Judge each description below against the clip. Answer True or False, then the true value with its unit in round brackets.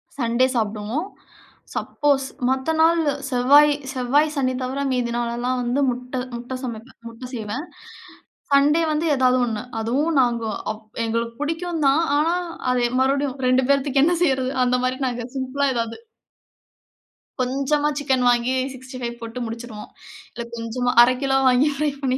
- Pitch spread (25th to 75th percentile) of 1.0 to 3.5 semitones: True (2.8 semitones)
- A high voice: True (255 Hz)